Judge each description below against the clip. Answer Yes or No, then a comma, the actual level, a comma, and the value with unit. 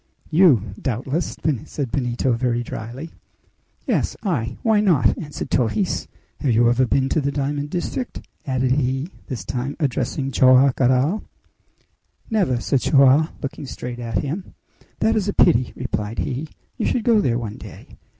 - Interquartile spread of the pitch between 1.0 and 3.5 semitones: No, average, 4.3 semitones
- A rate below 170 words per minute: Yes, average, 150 wpm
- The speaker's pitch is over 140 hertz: No, low, 135 Hz